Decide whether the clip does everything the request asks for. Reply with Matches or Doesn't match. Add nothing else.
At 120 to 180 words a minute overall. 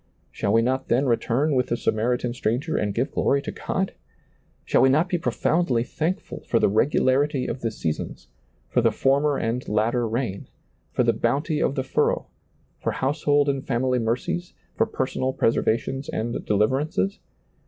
Matches